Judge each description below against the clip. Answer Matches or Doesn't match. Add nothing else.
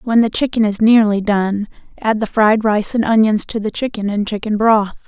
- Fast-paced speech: Matches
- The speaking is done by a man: Doesn't match